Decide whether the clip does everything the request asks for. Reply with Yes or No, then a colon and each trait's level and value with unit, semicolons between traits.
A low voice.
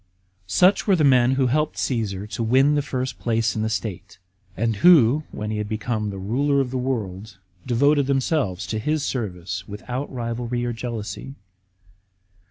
Yes: low, 120 Hz